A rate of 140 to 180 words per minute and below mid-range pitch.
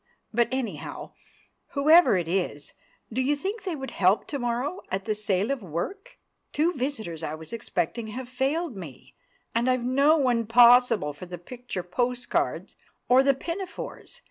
No: average, 165 wpm; high, 245 Hz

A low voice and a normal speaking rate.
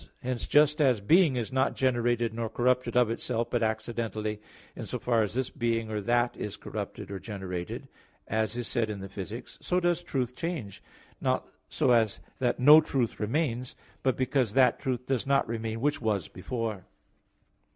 Yes: low, 120 Hz; average, 175 wpm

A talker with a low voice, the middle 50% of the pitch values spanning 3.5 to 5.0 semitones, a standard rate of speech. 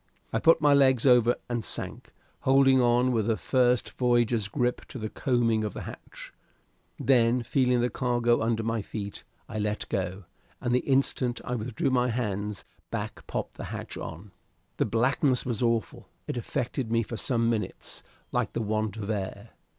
No: low, 120 Hz; narrow, 2.4 semitones; average, 175 wpm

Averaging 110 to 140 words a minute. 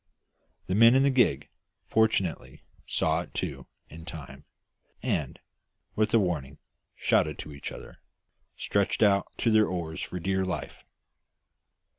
Yes: slow, 135 wpm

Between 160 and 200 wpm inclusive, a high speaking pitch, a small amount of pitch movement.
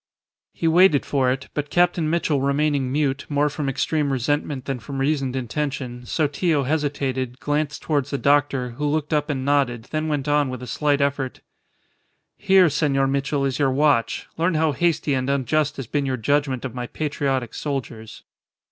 No: average, 175 wpm; medium, 140 Hz; narrow, 2.3 semitones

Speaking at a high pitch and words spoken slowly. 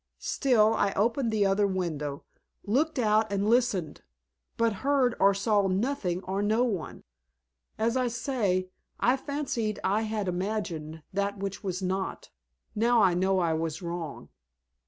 No: high, 200 Hz; average, 145 wpm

